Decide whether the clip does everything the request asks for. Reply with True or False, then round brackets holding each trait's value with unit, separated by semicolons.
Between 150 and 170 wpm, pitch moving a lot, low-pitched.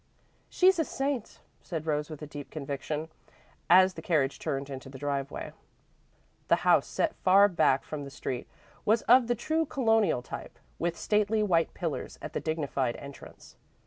False (160 wpm; 7.5 semitones; 165 Hz)